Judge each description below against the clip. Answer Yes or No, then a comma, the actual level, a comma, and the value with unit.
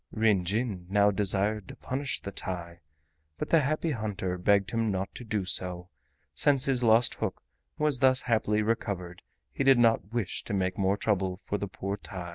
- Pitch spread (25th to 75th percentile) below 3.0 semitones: No, average, 3.9 semitones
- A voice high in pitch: No, low, 105 Hz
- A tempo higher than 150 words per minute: Yes, average, 185 wpm